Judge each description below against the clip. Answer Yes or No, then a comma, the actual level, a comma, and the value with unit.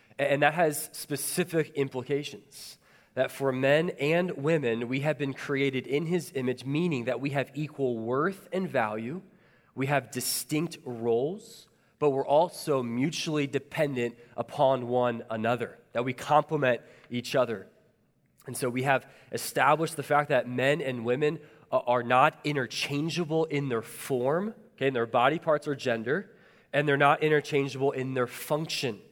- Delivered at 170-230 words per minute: No, average, 150 wpm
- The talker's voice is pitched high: No, medium, 140 Hz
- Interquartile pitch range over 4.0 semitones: No, average, 3.4 semitones